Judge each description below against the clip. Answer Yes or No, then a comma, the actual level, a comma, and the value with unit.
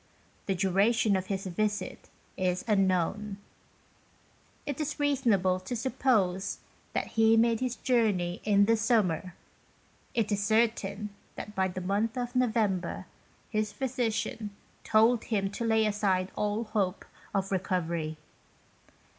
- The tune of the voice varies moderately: Yes, average, 3.2 semitones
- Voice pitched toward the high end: Yes, high, 210 Hz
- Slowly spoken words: Yes, slow, 130 wpm